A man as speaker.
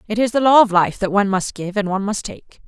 No: female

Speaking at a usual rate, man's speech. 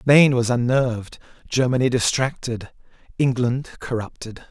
No: slow, 95 wpm; male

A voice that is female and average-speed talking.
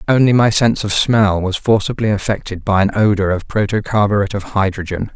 No: male; average, 175 wpm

